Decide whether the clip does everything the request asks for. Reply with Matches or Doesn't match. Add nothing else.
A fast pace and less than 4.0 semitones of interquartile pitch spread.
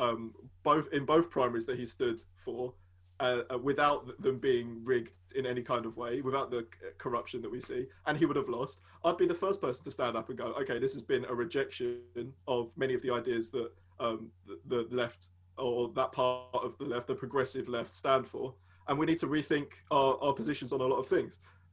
Matches